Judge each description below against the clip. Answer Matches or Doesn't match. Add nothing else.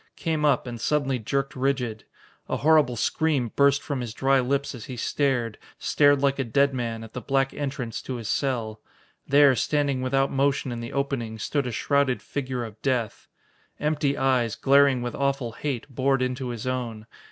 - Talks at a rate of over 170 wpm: Matches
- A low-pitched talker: Matches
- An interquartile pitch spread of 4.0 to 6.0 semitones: Doesn't match